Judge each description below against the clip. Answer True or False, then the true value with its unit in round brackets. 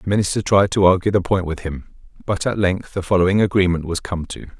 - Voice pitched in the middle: False (95 Hz)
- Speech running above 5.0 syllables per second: True (6.0 syllables/s)